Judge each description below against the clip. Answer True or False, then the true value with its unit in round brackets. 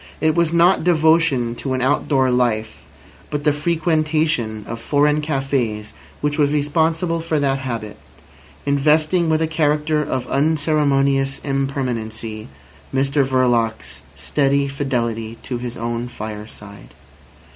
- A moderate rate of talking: False (120 wpm)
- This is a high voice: False (140 Hz)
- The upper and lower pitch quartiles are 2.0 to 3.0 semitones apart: False (4.2 semitones)